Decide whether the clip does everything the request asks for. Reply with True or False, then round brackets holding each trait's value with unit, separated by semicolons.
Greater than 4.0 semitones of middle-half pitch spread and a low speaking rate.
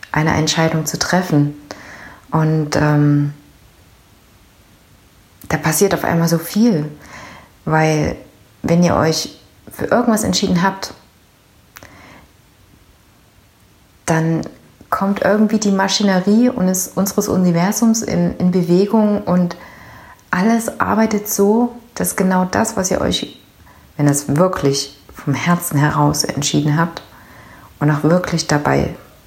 True (4.7 semitones; 110 wpm)